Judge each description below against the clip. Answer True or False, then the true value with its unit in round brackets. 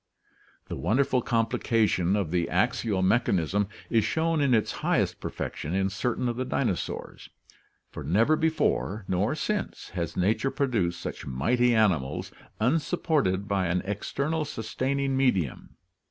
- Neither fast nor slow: False (130 wpm)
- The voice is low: True (110 Hz)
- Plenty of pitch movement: True (6.4 semitones)